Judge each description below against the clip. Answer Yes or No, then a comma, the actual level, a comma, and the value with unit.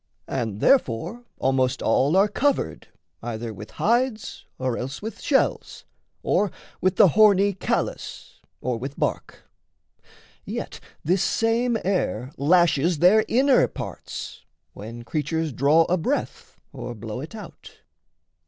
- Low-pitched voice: No, medium, 165 Hz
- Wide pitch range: Yes, wide, 8.8 semitones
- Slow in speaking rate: Yes, slow, 125 wpm